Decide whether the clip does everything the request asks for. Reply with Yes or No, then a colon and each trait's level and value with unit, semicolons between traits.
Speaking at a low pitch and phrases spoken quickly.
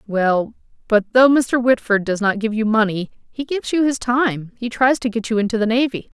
No: high, 230 Hz; fast, 225 wpm